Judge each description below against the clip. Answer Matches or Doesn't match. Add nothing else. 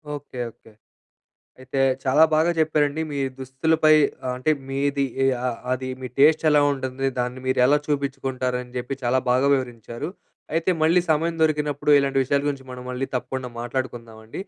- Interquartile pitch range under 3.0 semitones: Matches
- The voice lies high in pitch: Doesn't match